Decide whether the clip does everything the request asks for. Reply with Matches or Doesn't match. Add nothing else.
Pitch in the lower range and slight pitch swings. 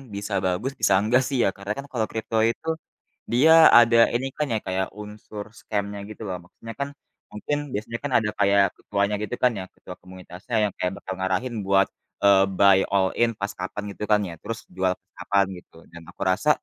Doesn't match